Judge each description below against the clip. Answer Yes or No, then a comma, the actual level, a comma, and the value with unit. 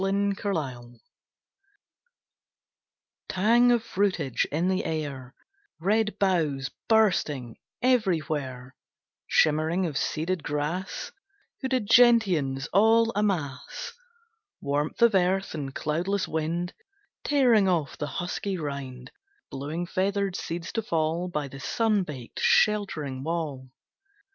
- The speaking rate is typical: No, slow, 105 wpm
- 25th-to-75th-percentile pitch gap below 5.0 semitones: No, wide, 5.6 semitones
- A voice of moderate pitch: Yes, medium, 170 Hz